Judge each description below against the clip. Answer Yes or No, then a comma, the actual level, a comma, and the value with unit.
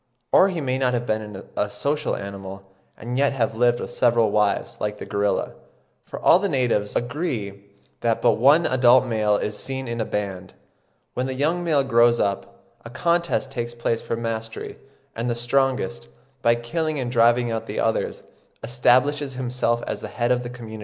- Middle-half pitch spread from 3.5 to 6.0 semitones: No, average, 3.1 semitones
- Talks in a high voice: No, low, 120 Hz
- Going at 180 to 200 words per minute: Yes, average, 185 wpm